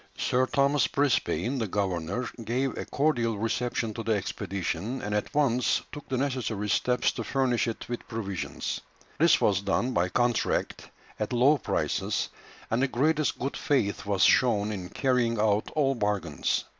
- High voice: No, low, 115 Hz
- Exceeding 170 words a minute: No, average, 160 wpm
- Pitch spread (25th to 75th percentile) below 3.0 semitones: No, average, 4.2 semitones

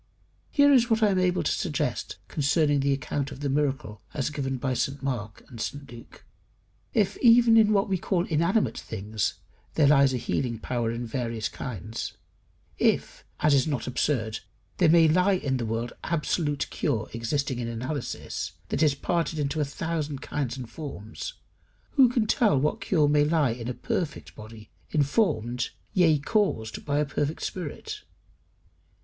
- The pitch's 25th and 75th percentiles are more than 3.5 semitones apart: Yes, wide, 5.5 semitones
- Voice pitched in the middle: Yes, medium, 145 Hz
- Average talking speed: Yes, average, 165 wpm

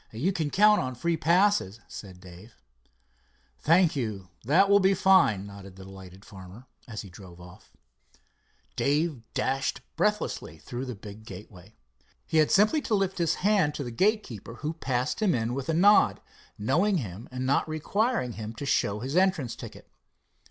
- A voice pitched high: No, low, 130 Hz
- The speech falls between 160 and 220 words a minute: Yes, average, 165 wpm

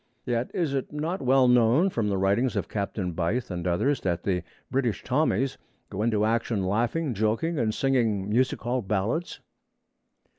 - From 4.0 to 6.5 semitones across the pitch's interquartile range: Yes, average, 4.9 semitones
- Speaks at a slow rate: No, average, 160 wpm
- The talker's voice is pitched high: No, low, 115 Hz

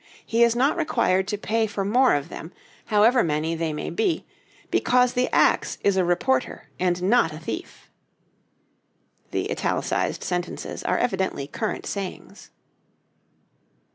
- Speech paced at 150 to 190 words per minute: No, average, 140 wpm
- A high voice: Yes, high, 200 Hz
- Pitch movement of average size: No, wide, 5.8 semitones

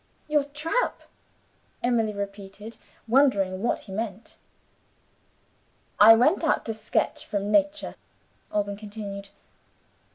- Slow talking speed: Yes, slow, 100 wpm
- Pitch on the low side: No, high, 220 Hz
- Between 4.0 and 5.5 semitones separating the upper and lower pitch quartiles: Yes, average, 5.1 semitones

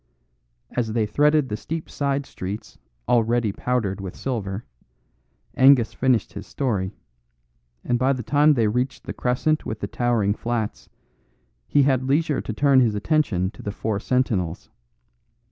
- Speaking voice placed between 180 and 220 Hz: No, low, 120 Hz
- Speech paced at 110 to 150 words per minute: Yes, average, 145 wpm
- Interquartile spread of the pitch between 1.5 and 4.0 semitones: No, average, 4.4 semitones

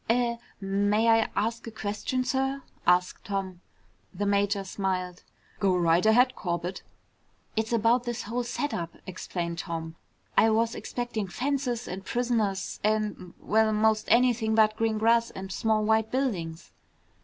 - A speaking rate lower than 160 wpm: Yes, average, 140 wpm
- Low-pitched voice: No, high, 215 Hz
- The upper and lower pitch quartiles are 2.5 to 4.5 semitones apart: Yes, average, 3.4 semitones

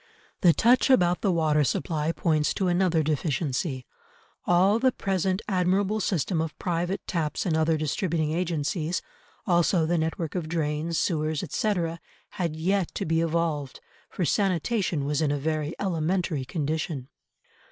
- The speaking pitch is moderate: Yes, medium, 165 Hz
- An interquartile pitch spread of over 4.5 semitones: No, average, 3.0 semitones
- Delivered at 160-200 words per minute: No, average, 140 wpm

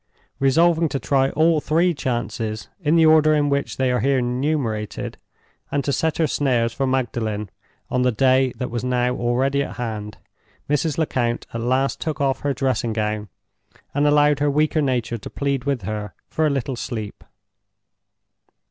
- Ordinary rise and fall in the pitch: Yes, average, 3.6 semitones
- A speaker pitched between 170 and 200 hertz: No, low, 135 Hz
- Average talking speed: Yes, average, 170 wpm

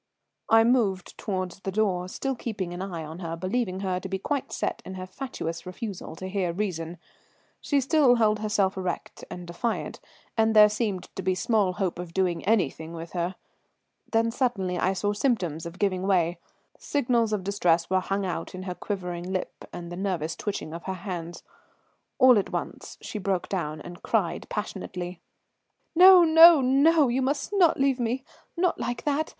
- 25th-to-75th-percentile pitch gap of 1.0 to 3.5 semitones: No, average, 4.5 semitones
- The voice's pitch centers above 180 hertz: Yes, high, 190 Hz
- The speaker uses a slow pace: No, average, 180 wpm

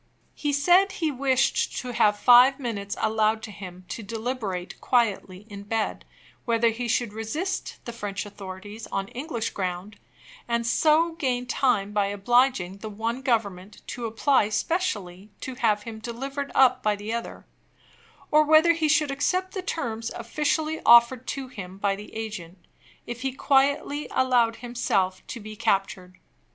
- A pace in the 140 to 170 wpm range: Yes, average, 150 wpm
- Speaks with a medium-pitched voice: No, high, 230 Hz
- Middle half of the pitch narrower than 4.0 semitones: No, average, 4.5 semitones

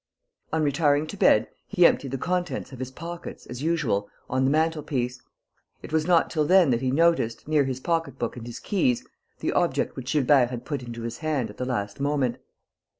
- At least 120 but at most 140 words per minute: No, fast, 205 wpm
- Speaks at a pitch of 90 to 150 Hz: Yes, medium, 140 Hz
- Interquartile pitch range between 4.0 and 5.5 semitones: Yes, average, 4.4 semitones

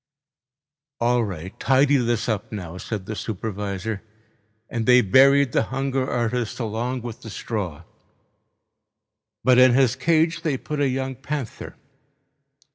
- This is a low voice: Yes, low, 120 Hz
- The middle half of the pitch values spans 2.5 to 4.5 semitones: Yes, average, 3.7 semitones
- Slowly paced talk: Yes, slow, 130 wpm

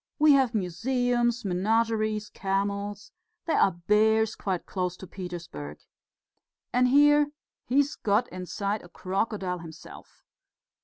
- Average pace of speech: No, slow, 110 wpm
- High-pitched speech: Yes, high, 210 Hz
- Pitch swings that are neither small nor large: Yes, average, 4.5 semitones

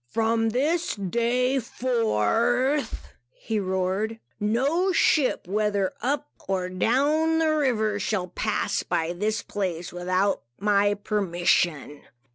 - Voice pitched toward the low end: No, high, 215 Hz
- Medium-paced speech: No, slow, 105 wpm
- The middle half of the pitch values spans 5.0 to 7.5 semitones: Yes, average, 5.3 semitones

